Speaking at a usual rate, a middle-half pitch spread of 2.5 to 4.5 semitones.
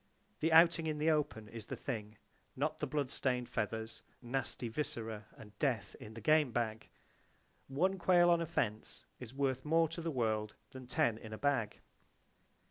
No: average, 170 wpm; wide, 5.6 semitones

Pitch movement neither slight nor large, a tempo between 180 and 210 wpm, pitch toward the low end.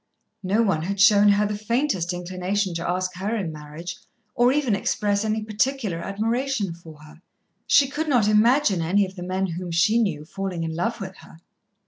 No: average, 3.7 semitones; average, 185 wpm; high, 195 Hz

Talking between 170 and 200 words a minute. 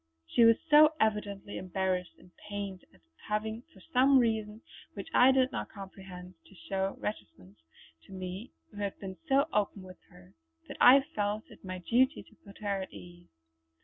Yes: average, 175 wpm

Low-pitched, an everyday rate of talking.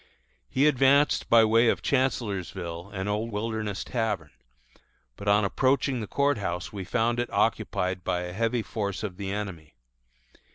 Yes: low, 105 Hz; average, 155 wpm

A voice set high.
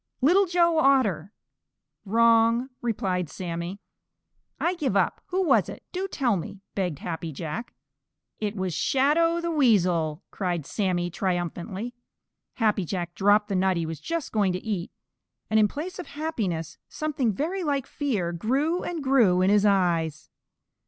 Yes: high, 210 Hz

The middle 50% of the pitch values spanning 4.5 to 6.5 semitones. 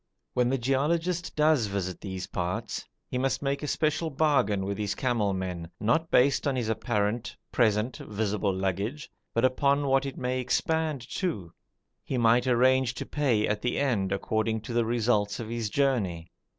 Yes: average, 4.8 semitones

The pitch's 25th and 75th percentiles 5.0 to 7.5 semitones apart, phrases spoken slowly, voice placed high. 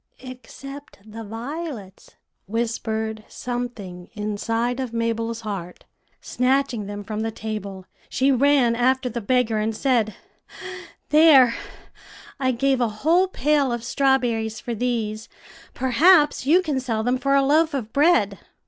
No: average, 3.8 semitones; slow, 130 wpm; high, 240 Hz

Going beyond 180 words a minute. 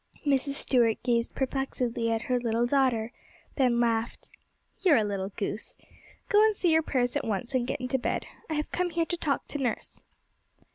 Yes: average, 190 wpm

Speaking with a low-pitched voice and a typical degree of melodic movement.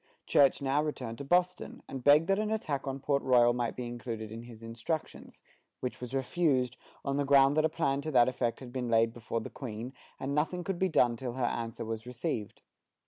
Yes: low, 130 Hz; average, 3.3 semitones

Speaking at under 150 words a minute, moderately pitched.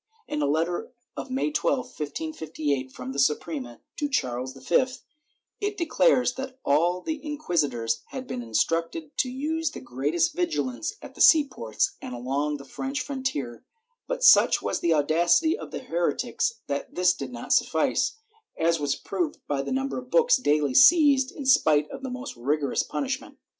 No: average, 170 wpm; medium, 175 Hz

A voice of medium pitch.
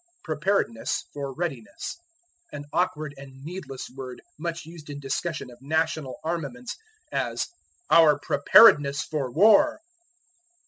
Yes: medium, 150 Hz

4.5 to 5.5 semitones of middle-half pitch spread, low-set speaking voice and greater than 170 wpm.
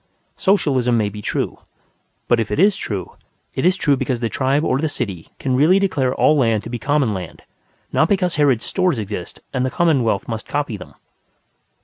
Yes: average, 5.1 semitones; low, 130 Hz; average, 195 wpm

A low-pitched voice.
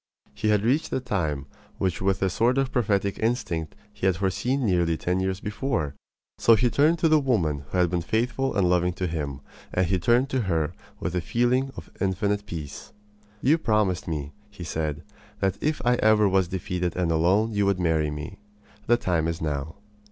Yes: very low, 95 Hz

